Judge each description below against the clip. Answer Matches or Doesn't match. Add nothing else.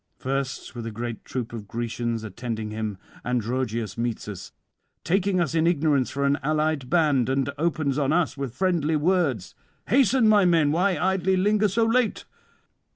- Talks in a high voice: Doesn't match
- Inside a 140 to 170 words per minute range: Matches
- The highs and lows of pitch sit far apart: Matches